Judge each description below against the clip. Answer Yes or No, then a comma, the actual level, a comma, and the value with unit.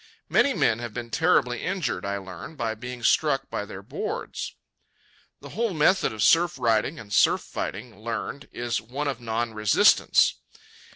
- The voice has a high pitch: No, low, 120 Hz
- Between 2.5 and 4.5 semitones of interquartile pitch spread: No, average, 5.1 semitones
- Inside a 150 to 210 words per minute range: Yes, average, 160 wpm